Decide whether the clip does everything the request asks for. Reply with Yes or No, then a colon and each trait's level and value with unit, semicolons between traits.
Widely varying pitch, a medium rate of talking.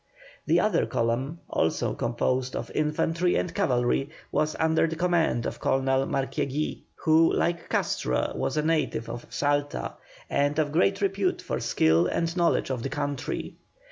No: average, 4.3 semitones; average, 150 wpm